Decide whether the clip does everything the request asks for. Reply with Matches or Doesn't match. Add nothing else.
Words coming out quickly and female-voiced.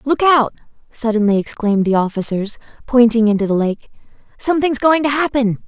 Doesn't match